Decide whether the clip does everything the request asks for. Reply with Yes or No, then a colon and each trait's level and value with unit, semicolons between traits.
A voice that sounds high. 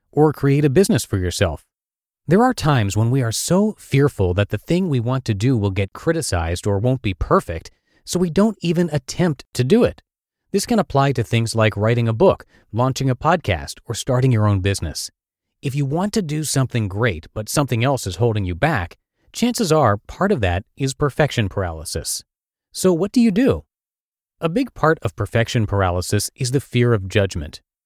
No: low, 125 Hz